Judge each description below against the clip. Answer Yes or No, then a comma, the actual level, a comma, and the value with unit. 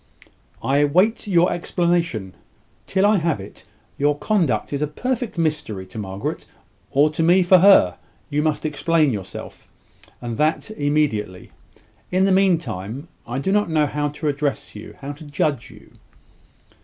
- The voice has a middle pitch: Yes, medium, 150 Hz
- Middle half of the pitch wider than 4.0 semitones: Yes, average, 4.6 semitones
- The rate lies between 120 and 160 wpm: Yes, average, 155 wpm